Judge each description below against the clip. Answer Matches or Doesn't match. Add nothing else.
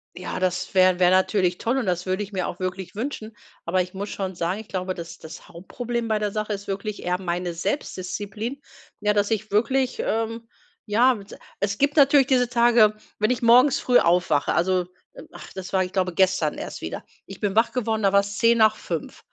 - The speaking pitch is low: Doesn't match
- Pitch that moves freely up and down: Doesn't match